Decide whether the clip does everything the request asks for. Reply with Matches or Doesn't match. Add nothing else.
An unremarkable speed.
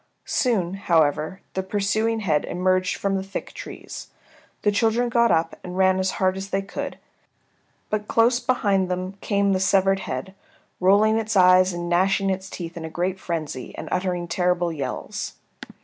Matches